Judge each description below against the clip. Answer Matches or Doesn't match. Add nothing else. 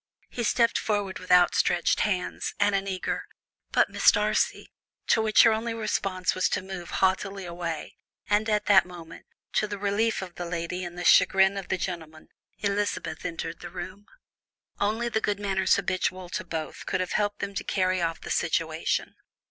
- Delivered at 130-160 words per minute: Doesn't match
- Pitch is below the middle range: Doesn't match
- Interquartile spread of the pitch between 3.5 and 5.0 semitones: Doesn't match